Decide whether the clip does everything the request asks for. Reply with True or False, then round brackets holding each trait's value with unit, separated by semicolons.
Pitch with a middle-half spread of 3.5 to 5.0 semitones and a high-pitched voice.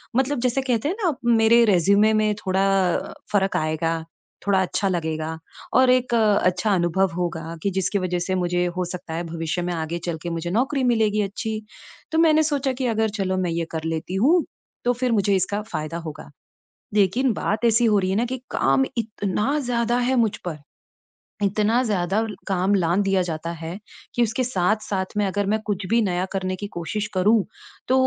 True (4.3 semitones; 200 Hz)